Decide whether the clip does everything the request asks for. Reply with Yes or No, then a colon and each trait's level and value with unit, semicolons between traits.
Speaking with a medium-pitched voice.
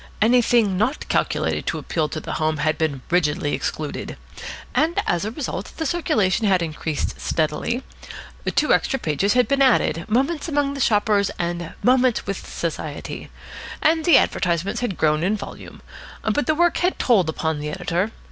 No: high, 200 Hz